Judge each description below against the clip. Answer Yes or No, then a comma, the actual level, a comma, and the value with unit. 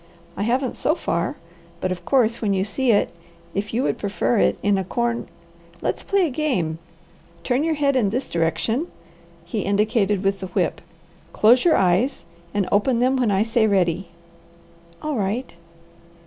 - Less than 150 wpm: No, average, 170 wpm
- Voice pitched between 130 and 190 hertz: No, high, 220 Hz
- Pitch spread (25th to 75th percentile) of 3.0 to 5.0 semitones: Yes, average, 4.7 semitones